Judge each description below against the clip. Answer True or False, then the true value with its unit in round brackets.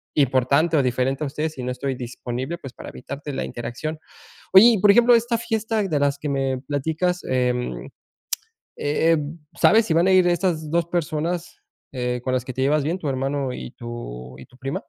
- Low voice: False (145 Hz)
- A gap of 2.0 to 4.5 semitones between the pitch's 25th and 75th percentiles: False (5.1 semitones)